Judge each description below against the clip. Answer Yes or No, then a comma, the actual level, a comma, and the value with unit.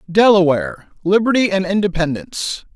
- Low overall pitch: No, high, 190 Hz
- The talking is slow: Yes, slow, 65 wpm